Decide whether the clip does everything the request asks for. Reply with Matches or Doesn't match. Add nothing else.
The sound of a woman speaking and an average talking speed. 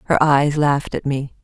Doesn't match